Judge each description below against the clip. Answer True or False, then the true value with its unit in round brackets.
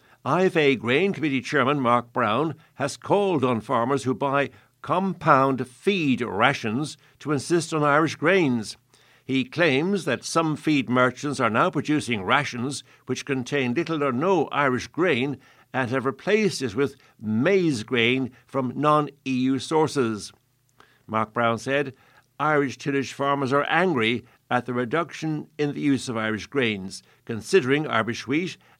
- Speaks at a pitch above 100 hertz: True (135 Hz)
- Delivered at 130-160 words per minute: True (140 wpm)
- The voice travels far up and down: False (3.4 semitones)